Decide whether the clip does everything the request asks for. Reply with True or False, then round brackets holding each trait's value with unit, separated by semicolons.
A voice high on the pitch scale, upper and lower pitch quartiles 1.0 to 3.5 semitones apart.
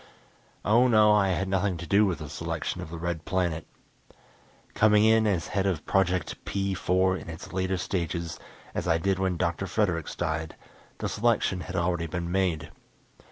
False (90 Hz; 2.6 semitones)